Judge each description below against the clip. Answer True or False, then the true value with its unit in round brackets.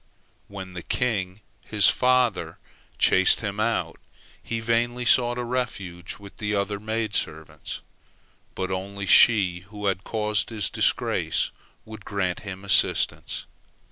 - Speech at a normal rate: False (130 wpm)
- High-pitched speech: False (105 Hz)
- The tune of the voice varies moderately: True (3.1 semitones)